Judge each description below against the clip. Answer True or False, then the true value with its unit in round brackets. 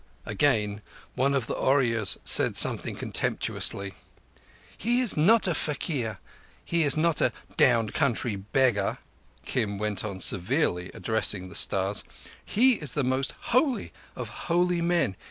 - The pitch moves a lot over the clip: True (7.9 semitones)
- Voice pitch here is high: False (130 Hz)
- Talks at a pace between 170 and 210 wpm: False (135 wpm)